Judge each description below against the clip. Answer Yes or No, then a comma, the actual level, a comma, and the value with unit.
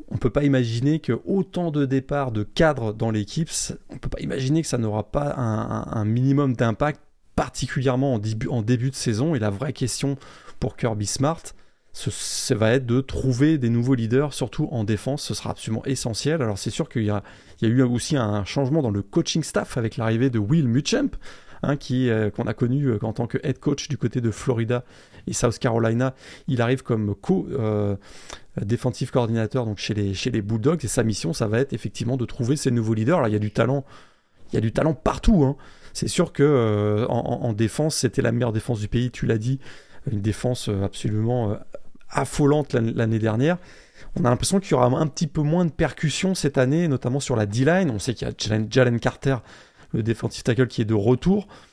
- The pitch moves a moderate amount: Yes, average, 3.8 semitones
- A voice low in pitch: Yes, low, 125 Hz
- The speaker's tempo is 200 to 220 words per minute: Yes, average, 215 wpm